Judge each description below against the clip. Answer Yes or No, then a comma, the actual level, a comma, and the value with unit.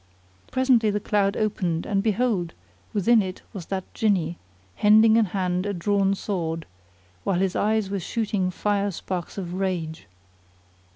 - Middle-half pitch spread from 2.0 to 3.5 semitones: Yes, average, 2.7 semitones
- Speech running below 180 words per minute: Yes, average, 140 wpm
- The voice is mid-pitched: No, high, 195 Hz